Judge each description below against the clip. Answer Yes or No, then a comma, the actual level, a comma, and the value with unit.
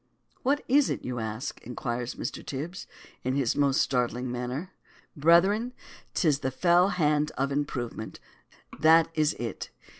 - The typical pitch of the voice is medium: Yes, medium, 145 Hz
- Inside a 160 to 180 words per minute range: No, average, 145 wpm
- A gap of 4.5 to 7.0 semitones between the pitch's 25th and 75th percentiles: Yes, wide, 5.4 semitones